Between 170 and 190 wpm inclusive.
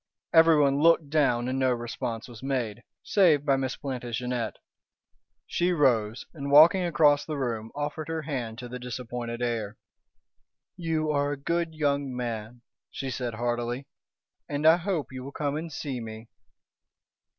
No: average, 150 wpm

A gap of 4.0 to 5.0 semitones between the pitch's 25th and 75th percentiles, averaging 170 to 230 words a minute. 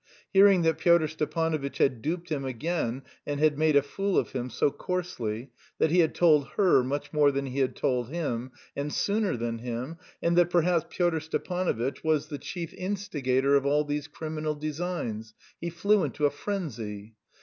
Yes: average, 4.4 semitones; average, 180 wpm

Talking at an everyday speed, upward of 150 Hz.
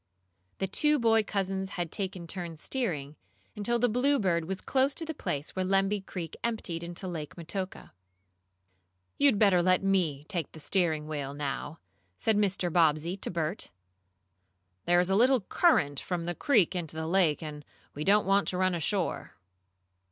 Yes: average, 165 wpm; medium, 185 Hz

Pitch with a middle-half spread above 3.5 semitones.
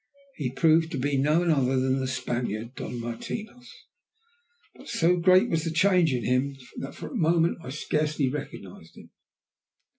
Yes: average, 4.4 semitones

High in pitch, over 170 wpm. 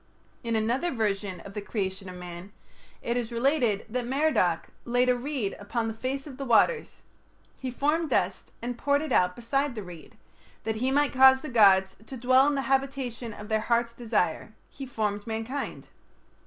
Yes: high, 235 Hz; average, 180 wpm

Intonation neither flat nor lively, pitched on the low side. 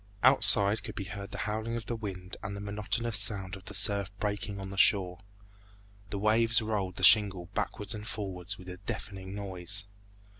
No: narrow, 1.9 semitones; low, 100 Hz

